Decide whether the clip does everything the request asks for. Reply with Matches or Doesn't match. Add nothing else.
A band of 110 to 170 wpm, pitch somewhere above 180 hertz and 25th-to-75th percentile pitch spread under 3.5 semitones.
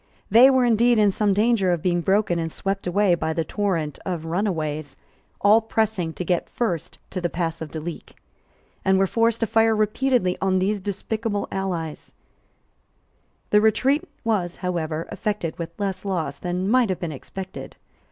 Doesn't match